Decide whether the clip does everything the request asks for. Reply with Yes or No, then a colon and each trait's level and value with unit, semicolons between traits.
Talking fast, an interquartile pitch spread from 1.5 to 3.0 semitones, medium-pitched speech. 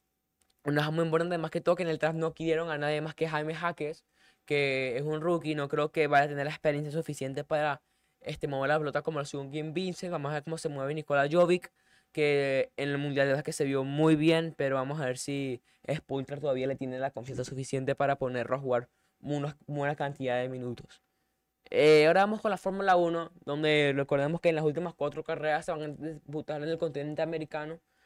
Yes: fast, 220 wpm; narrow, 2.4 semitones; medium, 150 Hz